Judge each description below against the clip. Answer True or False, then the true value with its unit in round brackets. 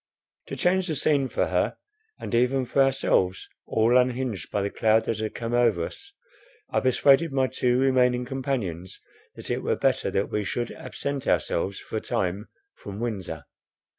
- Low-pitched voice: True (120 Hz)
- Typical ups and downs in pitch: True (4.5 semitones)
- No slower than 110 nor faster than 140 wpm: False (170 wpm)